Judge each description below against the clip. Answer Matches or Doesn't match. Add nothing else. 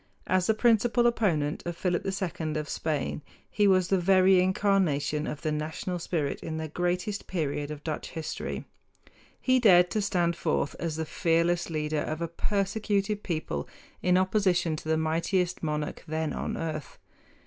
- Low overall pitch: Doesn't match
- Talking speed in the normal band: Matches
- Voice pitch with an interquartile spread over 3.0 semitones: Matches